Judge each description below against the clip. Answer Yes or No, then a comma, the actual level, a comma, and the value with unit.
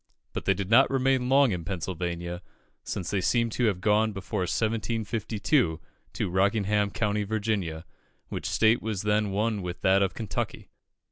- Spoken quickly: No, average, 155 wpm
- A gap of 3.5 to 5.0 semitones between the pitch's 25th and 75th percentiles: No, average, 3.1 semitones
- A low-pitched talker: Yes, low, 105 Hz